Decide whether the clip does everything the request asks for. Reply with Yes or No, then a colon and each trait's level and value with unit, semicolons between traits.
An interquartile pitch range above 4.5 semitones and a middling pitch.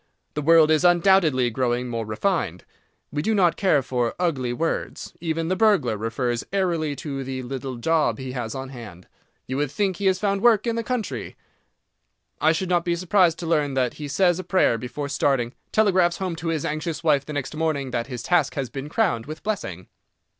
Yes: wide, 5.5 semitones; medium, 150 Hz